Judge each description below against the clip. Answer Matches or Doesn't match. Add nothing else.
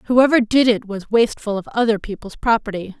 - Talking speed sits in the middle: Matches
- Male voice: Doesn't match